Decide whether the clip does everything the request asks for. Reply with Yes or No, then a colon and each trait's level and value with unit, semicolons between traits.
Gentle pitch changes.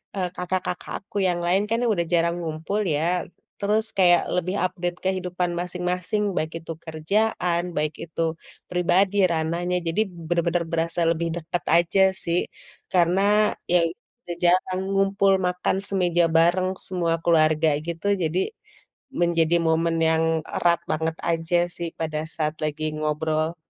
Yes: narrow, 2.0 semitones